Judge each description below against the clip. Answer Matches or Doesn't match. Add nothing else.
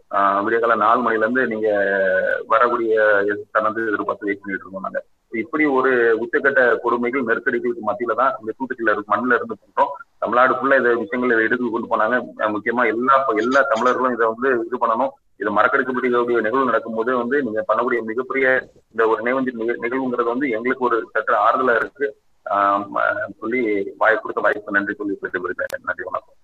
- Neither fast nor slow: Doesn't match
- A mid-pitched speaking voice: Doesn't match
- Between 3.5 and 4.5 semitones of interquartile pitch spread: Doesn't match